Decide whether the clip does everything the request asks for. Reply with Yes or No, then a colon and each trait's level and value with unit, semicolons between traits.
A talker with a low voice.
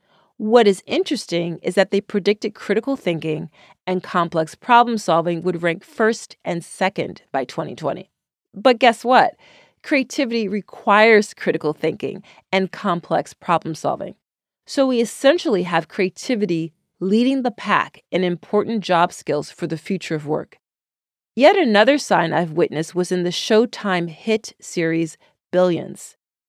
No: high, 190 Hz